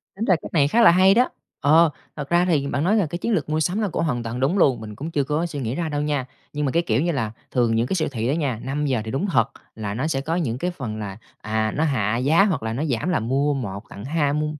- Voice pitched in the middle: Yes, medium, 145 Hz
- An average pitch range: No, wide, 5.7 semitones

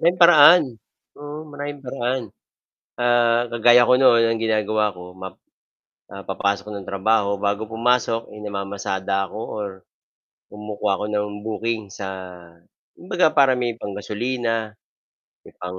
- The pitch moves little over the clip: No, average, 3.4 semitones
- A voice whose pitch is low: Yes, low, 110 Hz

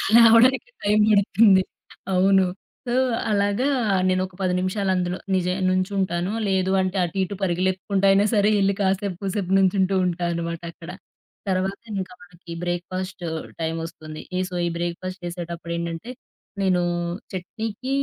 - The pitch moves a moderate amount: No, narrow, 2.1 semitones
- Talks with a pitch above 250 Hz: No, medium, 185 Hz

